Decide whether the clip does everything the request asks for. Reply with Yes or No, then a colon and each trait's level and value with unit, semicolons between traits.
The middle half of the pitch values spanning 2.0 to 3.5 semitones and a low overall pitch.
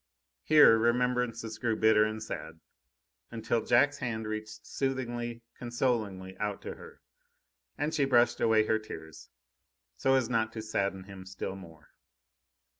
Yes: narrow, 2.4 semitones; low, 110 Hz